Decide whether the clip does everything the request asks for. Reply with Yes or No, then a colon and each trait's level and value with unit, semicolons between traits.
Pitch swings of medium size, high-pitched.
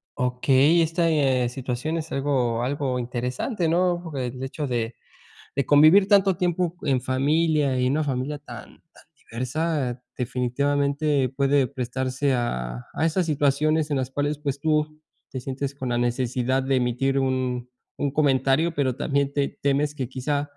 No: average, 3.1 semitones; medium, 140 Hz